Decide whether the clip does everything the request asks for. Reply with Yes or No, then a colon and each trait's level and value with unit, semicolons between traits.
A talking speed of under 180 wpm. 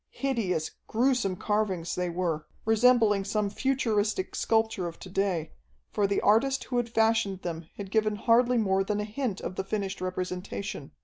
Yes: average, 165 wpm